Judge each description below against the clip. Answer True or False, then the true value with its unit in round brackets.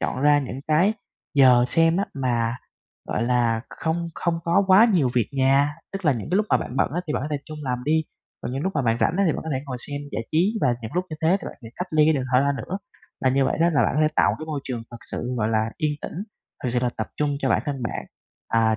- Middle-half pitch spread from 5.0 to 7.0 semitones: False (4.5 semitones)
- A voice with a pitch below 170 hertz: True (140 Hz)